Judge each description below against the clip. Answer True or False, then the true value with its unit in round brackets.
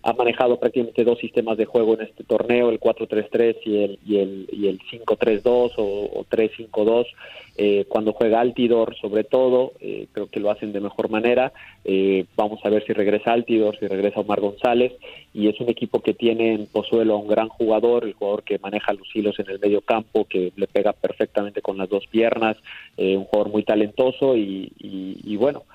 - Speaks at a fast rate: True (200 wpm)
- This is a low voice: True (110 Hz)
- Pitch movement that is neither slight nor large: False (2.3 semitones)